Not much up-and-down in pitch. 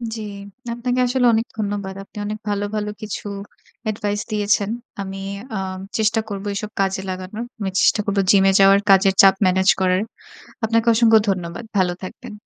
Yes: narrow, 2.2 semitones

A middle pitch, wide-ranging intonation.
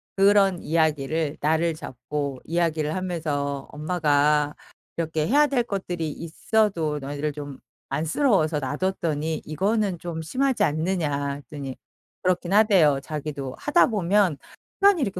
No: medium, 160 Hz; average, 4.3 semitones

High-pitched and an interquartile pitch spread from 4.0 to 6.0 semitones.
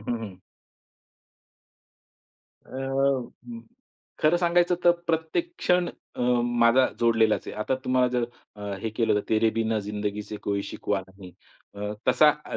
No: low, 120 Hz; average, 4.6 semitones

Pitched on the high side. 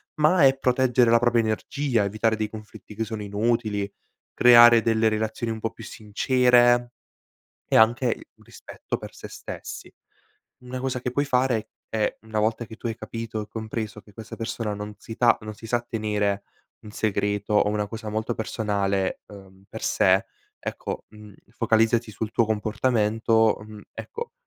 No: low, 110 Hz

